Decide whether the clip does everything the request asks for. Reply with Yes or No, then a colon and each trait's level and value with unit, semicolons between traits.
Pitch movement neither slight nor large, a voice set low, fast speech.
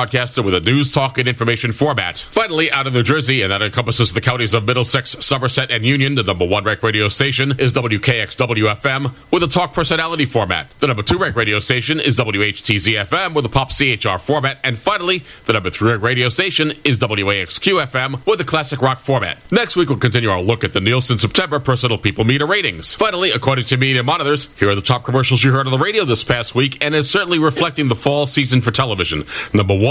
Yes: average, 3.8 semitones; low, 130 Hz; fast, 215 wpm